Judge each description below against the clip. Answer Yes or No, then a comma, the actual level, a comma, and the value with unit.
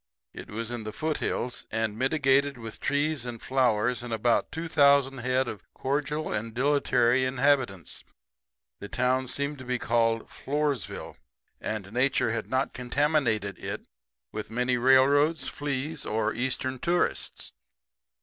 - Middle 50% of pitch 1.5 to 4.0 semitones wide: Yes, average, 3.5 semitones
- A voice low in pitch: Yes, low, 130 Hz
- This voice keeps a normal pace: No, slow, 130 wpm